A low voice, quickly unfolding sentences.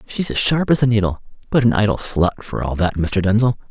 Yes: low, 110 Hz; fast, 245 wpm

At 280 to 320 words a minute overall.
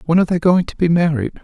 Yes: fast, 290 wpm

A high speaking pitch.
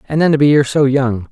No: medium, 140 Hz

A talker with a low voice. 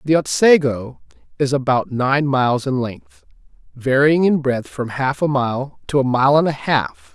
Yes: low, 130 Hz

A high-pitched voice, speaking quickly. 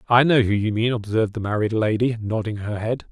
No: low, 110 Hz; fast, 230 wpm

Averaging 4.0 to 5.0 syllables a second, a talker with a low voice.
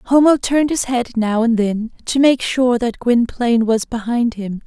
No: 4.5 syllables/s; high, 240 Hz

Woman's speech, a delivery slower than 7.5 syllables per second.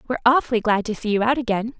No: female; 7.8 syllables/s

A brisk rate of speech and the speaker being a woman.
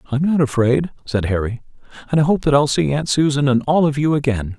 No: fast, 235 wpm; male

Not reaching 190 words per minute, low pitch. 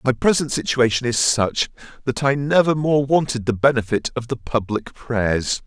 Yes: average, 170 wpm; low, 125 Hz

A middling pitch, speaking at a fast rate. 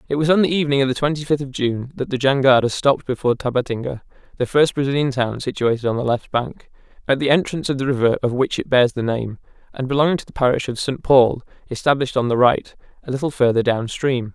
No: low, 130 Hz; fast, 230 wpm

